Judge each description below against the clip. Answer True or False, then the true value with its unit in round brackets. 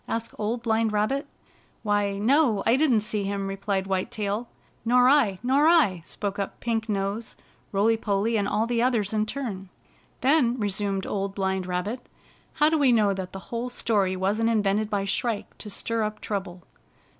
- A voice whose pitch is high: True (215 Hz)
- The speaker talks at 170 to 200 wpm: True (185 wpm)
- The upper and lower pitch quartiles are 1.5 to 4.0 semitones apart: True (3.0 semitones)